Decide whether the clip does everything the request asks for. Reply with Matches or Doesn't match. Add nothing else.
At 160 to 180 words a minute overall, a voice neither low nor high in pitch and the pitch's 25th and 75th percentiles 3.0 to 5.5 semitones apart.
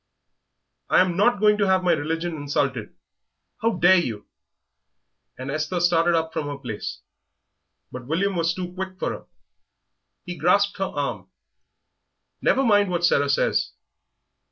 Doesn't match